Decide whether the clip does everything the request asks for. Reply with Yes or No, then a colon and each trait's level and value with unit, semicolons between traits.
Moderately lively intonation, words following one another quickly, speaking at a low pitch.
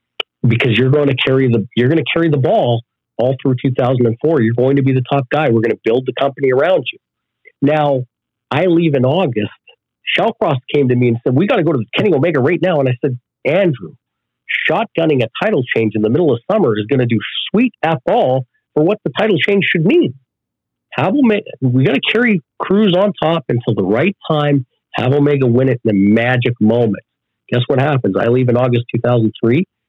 Yes: average, 4.0 semitones; fast, 215 wpm; low, 130 Hz